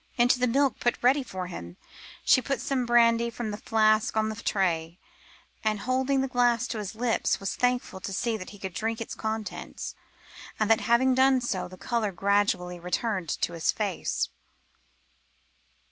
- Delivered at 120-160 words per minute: No, average, 175 wpm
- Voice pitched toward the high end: Yes, high, 220 Hz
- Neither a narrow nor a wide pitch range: Yes, average, 3.8 semitones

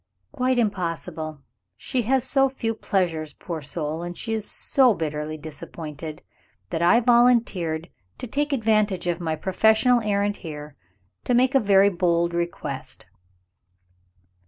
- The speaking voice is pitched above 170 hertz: Yes, medium, 185 Hz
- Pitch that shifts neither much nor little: No, wide, 6.5 semitones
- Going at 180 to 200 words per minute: No, slow, 135 wpm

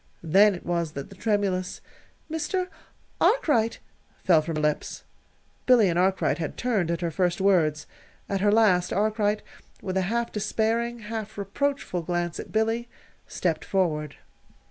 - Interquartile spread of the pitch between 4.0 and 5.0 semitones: Yes, average, 4.3 semitones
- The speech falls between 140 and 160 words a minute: Yes, average, 145 wpm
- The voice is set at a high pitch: Yes, high, 195 Hz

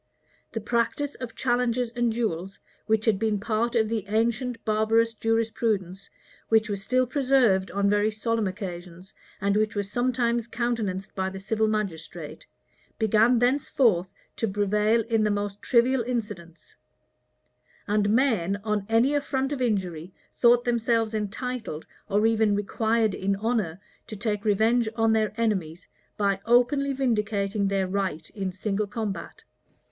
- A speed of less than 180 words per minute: Yes, average, 140 wpm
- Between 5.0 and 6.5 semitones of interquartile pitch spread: No, average, 2.8 semitones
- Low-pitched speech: No, high, 220 Hz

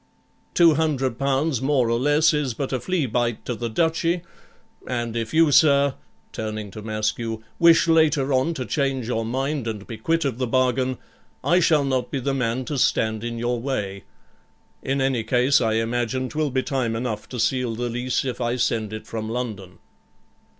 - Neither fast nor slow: Yes, average, 185 wpm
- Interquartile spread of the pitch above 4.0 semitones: No, average, 3.5 semitones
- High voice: No, low, 125 Hz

